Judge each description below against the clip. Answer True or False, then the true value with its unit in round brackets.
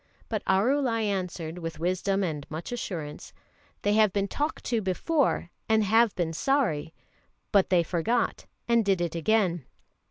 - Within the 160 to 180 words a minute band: False (150 wpm)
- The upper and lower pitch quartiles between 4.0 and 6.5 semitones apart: True (4.8 semitones)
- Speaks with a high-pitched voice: True (195 Hz)